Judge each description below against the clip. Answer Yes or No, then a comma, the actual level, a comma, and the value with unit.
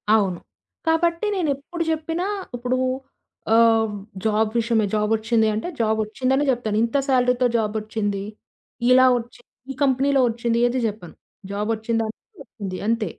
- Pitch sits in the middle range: No, high, 230 Hz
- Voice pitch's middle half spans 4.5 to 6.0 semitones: No, average, 3.1 semitones